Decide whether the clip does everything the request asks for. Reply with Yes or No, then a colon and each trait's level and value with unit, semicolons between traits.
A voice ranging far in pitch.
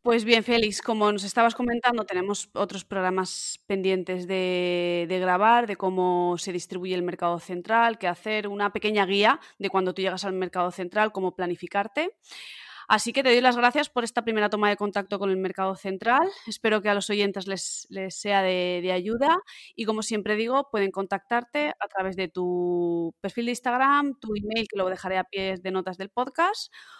No: average, 3.5 semitones